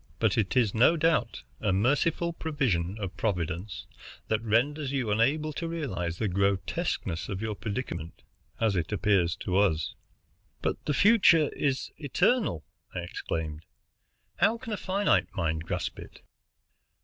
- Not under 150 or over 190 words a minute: No, average, 140 wpm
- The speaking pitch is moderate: No, low, 110 Hz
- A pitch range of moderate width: No, wide, 8.3 semitones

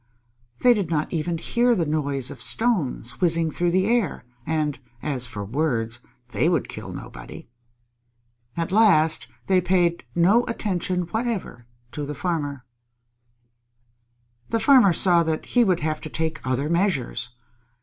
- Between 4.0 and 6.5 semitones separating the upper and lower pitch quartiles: Yes, average, 4.4 semitones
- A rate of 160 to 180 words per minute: No, average, 140 wpm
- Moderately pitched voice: Yes, medium, 165 Hz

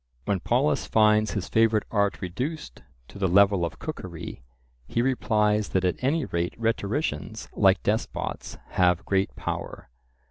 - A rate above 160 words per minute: No, average, 140 wpm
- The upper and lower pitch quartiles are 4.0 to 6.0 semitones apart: No, average, 3.6 semitones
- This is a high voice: No, low, 105 Hz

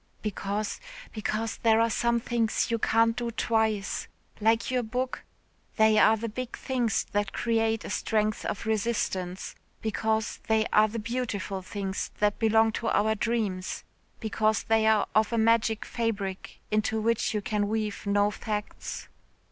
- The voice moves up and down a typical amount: No, narrow, 1.5 semitones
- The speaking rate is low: No, average, 150 wpm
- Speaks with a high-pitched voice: Yes, high, 220 Hz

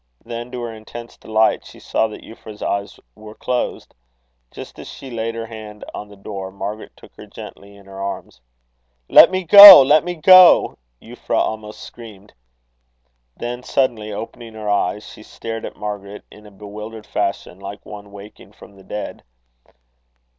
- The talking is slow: No, average, 165 wpm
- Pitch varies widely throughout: No, narrow, 2.4 semitones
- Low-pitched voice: Yes, low, 110 Hz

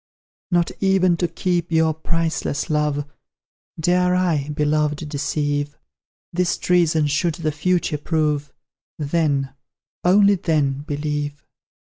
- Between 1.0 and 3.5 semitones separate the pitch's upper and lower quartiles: Yes, average, 2.9 semitones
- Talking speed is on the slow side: Yes, slow, 105 wpm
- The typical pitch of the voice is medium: Yes, medium, 155 Hz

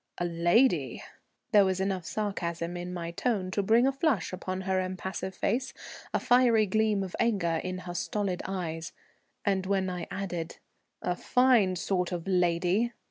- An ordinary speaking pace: Yes, average, 160 wpm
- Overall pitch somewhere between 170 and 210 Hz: Yes, medium, 185 Hz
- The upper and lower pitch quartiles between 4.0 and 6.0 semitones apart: No, average, 3.1 semitones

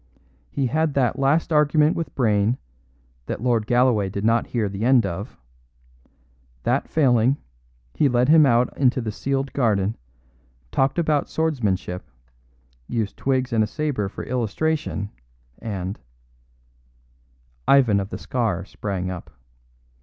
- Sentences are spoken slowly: Yes, slow, 130 wpm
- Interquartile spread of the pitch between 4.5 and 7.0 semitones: Yes, wide, 5.4 semitones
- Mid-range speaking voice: No, low, 120 Hz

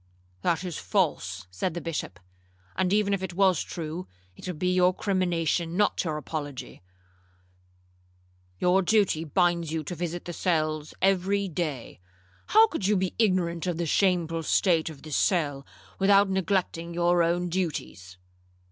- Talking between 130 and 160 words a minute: Yes, average, 150 wpm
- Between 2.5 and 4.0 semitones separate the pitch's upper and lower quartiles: Yes, average, 2.9 semitones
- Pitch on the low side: No, medium, 175 Hz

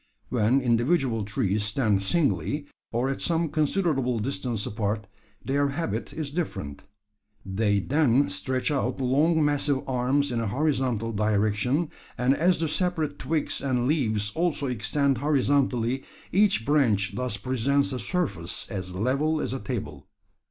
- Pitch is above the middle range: No, low, 130 Hz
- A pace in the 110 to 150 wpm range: Yes, average, 140 wpm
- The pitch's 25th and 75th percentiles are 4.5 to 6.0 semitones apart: Yes, average, 5.1 semitones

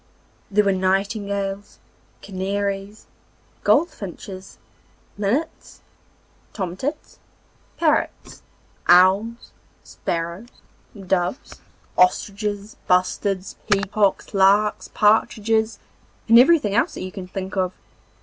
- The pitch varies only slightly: Yes, narrow, 2.3 semitones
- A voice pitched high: Yes, high, 200 Hz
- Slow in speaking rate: Yes, slow, 80 wpm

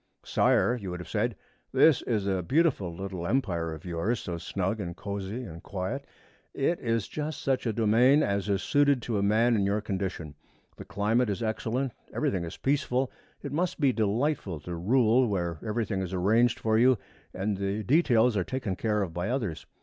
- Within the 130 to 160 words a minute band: No, average, 190 wpm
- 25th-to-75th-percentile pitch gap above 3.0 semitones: Yes, average, 4.7 semitones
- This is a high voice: No, low, 105 Hz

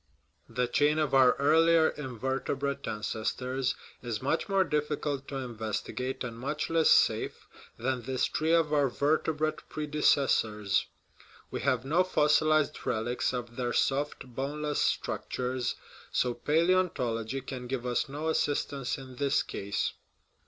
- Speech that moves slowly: Yes, slow, 130 wpm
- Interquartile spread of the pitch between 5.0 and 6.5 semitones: No, average, 3.3 semitones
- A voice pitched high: No, low, 135 Hz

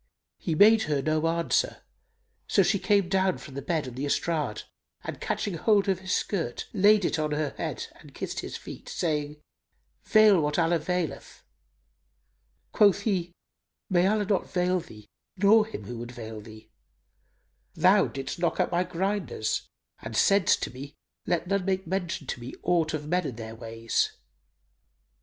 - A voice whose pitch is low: No, medium, 170 Hz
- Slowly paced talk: No, average, 165 wpm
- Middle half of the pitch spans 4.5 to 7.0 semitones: Yes, average, 5.1 semitones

